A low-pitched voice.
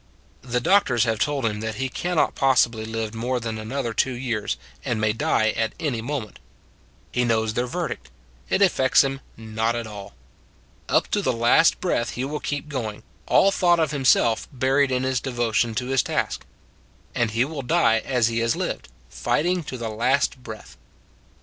Yes: low, 120 Hz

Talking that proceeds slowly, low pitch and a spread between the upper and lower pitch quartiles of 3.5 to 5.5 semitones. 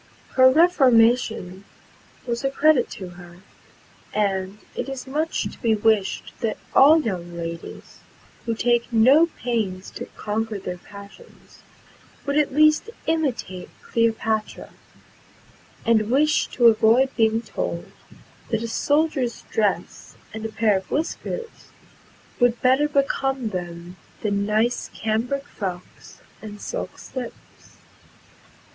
No: slow, 120 wpm; high, 230 Hz; average, 4.7 semitones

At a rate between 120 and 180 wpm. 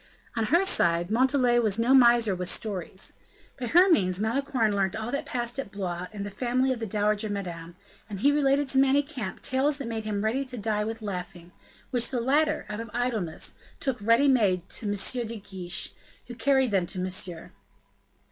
No: average, 190 wpm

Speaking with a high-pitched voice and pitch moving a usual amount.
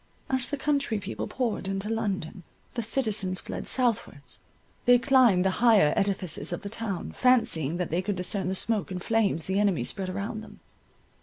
Yes: high, 200 Hz; average, 3.8 semitones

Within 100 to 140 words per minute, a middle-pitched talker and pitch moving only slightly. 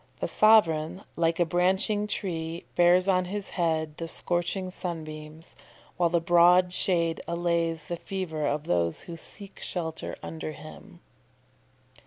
Yes: slow, 135 wpm; medium, 170 Hz; narrow, 2.1 semitones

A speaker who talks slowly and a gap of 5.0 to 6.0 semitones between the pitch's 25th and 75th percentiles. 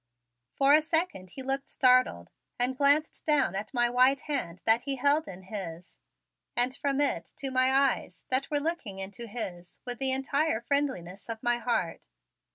No: average, 170 wpm; wide, 5.6 semitones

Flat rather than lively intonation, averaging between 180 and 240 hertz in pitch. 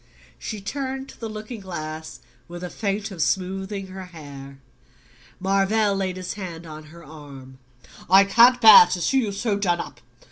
No: average, 4.3 semitones; high, 190 Hz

